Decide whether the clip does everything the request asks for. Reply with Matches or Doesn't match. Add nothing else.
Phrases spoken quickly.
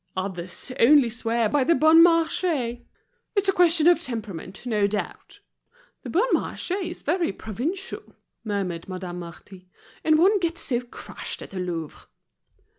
Doesn't match